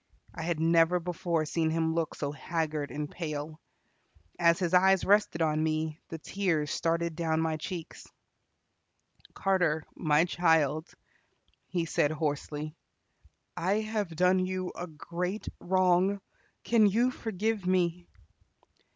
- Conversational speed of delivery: No, slow, 125 wpm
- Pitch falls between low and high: Yes, medium, 170 Hz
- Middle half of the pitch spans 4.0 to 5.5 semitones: No, average, 2.7 semitones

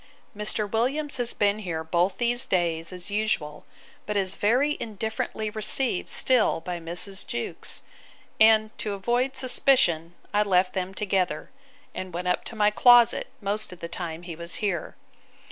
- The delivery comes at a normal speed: Yes, average, 155 wpm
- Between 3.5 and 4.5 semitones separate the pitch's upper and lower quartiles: Yes, average, 4.0 semitones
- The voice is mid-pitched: No, high, 200 Hz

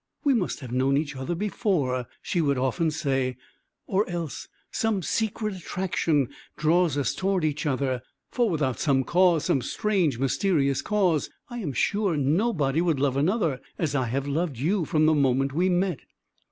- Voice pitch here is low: No, medium, 155 Hz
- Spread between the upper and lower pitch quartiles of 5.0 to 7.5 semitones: Yes, average, 5.3 semitones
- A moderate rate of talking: Yes, average, 165 wpm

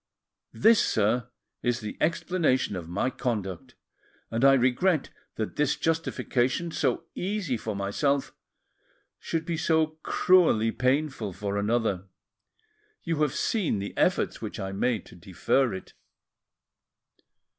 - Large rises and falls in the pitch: Yes, wide, 7.1 semitones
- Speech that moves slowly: Yes, slow, 125 wpm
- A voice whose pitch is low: Yes, low, 125 Hz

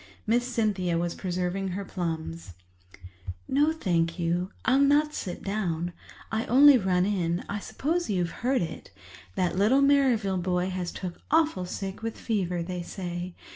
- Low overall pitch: No, high, 190 Hz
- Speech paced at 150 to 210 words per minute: No, average, 140 wpm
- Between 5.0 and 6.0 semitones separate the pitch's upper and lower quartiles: Yes, average, 5.3 semitones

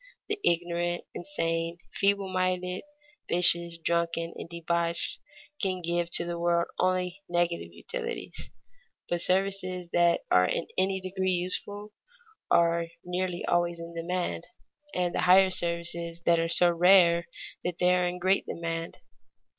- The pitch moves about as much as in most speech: No, narrow, 1.4 semitones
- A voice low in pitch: No, medium, 175 Hz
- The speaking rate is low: Yes, slow, 130 wpm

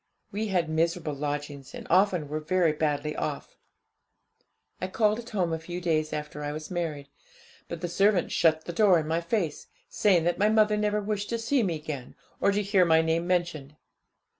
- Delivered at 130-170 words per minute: No, average, 190 wpm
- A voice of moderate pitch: Yes, medium, 170 Hz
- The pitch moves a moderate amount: Yes, average, 4.4 semitones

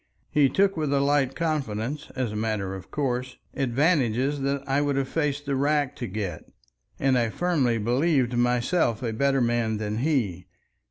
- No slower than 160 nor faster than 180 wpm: Yes, average, 170 wpm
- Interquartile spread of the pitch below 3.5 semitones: No, average, 3.9 semitones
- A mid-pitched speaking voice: No, low, 130 Hz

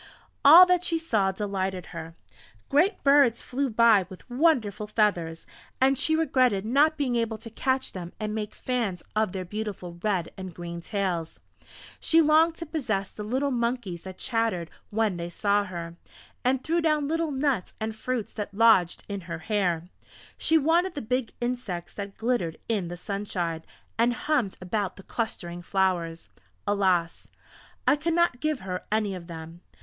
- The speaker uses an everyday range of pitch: No, wide, 6.2 semitones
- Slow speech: No, average, 165 wpm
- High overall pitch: Yes, high, 215 Hz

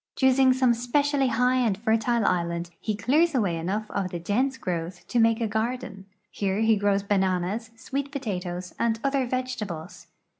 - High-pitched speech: Yes, high, 225 Hz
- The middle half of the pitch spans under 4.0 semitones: No, average, 5.0 semitones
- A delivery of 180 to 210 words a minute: No, average, 160 wpm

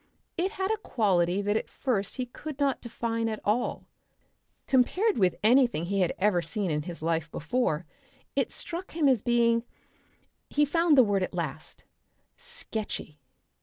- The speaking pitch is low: No, high, 230 Hz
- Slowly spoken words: No, average, 160 wpm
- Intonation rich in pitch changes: Yes, wide, 6.6 semitones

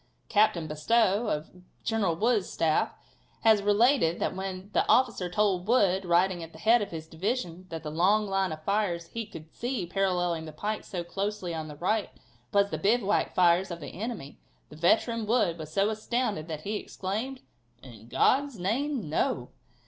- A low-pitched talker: No, high, 195 Hz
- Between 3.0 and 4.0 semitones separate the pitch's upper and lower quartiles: No, average, 4.4 semitones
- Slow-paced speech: No, average, 175 wpm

